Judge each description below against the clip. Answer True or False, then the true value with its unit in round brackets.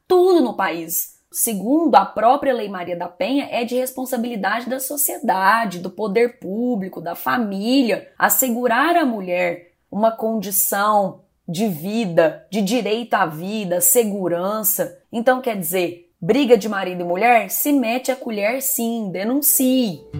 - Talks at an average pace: True (135 wpm)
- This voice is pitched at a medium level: False (225 Hz)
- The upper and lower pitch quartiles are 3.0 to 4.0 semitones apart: False (5.4 semitones)